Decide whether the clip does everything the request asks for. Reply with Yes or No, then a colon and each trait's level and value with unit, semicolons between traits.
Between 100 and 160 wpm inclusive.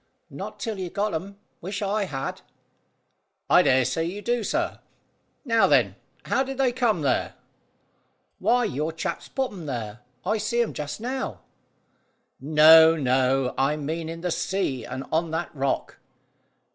Yes: average, 155 wpm